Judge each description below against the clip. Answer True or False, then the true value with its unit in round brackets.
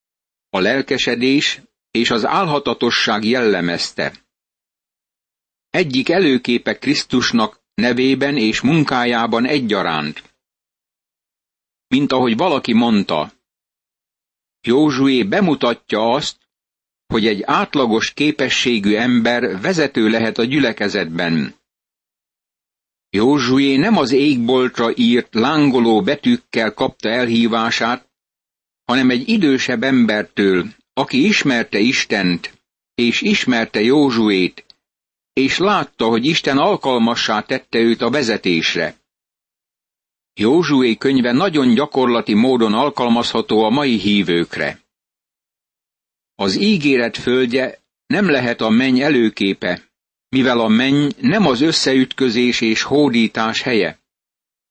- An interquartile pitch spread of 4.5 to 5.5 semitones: False (3.4 semitones)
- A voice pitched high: False (125 Hz)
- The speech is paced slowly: True (90 wpm)